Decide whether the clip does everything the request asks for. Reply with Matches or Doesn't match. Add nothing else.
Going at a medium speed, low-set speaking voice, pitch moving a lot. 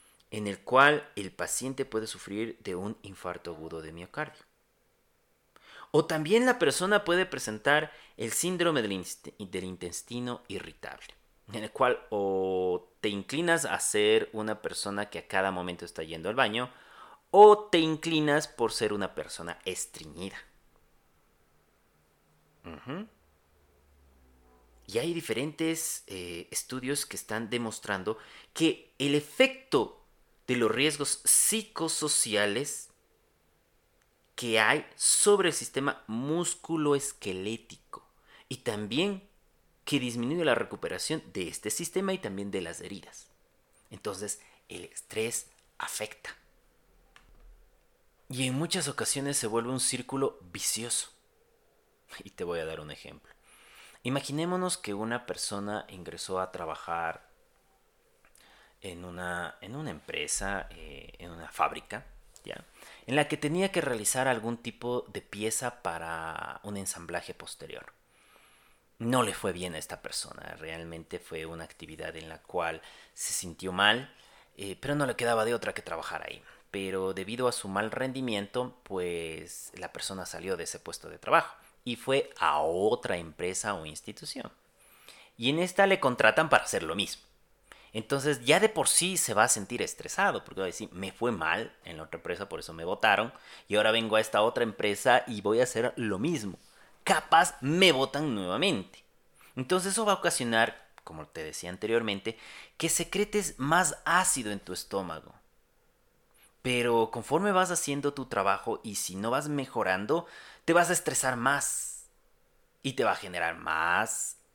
Matches